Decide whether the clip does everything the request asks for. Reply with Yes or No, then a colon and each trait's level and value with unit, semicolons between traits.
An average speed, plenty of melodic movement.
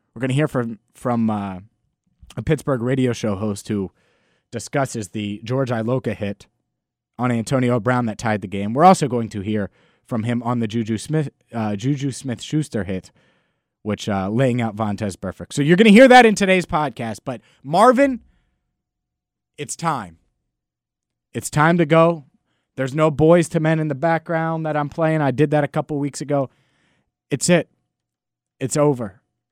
Yes: average, 175 wpm; wide, 6.3 semitones